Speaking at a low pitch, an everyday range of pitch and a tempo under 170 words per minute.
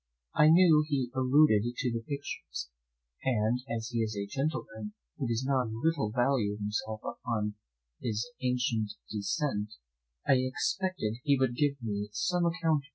Yes: low, 125 Hz; average, 4.8 semitones; average, 160 wpm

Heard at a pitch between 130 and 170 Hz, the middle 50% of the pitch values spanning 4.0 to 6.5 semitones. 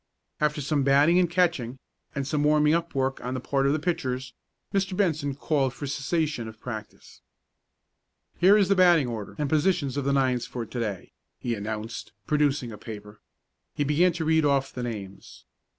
Yes: medium, 140 Hz; average, 4.3 semitones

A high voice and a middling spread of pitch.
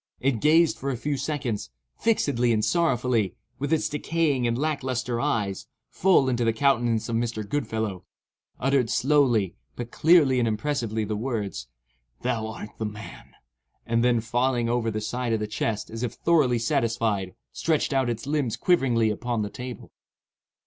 No: low, 120 Hz; average, 3.7 semitones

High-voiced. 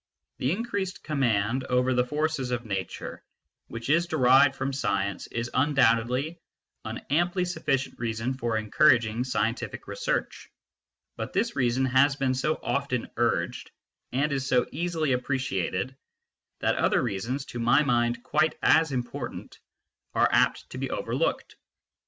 No: low, 130 Hz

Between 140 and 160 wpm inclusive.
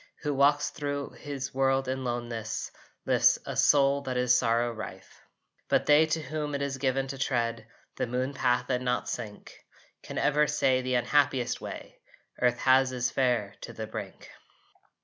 No: average, 170 wpm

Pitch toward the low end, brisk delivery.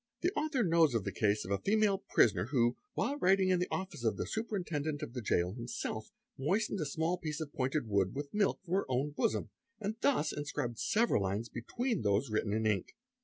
No: medium, 145 Hz; fast, 220 wpm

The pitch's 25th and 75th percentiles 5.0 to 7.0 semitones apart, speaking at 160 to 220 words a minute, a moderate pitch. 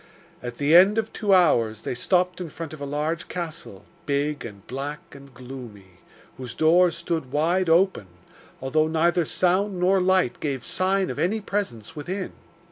Yes: wide, 5.4 semitones; average, 165 wpm; medium, 160 Hz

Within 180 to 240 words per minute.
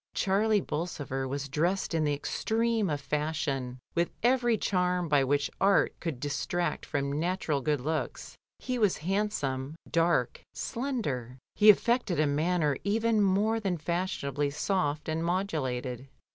No: average, 140 wpm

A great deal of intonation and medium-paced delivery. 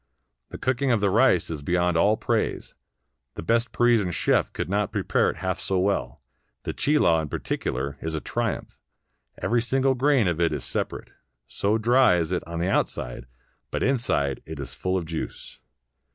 Yes: wide, 6.3 semitones; average, 180 wpm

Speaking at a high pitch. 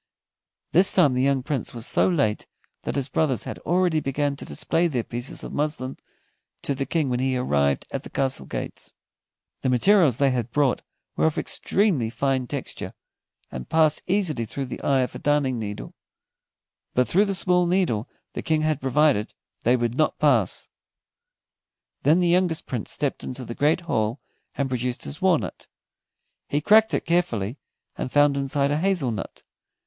No: medium, 140 Hz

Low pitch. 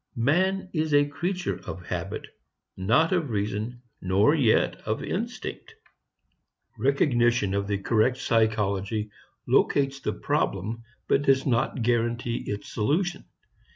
Yes: low, 120 Hz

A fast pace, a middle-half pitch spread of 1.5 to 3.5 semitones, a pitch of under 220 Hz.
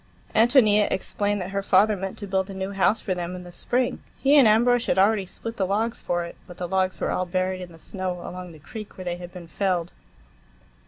Yes: fast, 235 wpm; average, 2.8 semitones; high, 190 Hz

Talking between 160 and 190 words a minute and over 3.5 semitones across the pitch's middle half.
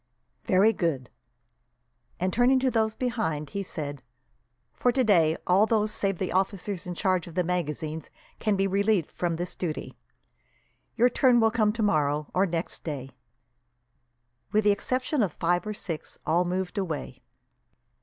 No: average, 150 wpm; average, 4.5 semitones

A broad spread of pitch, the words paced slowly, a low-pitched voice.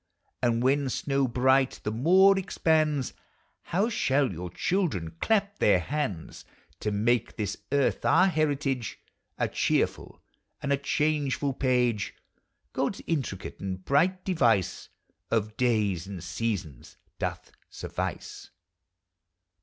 Yes: wide, 6.2 semitones; slow, 115 wpm; low, 130 Hz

